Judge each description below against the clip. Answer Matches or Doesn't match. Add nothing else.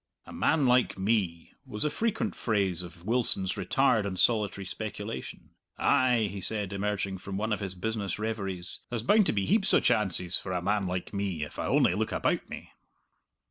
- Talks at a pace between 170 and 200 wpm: Matches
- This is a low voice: Matches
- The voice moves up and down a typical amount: Matches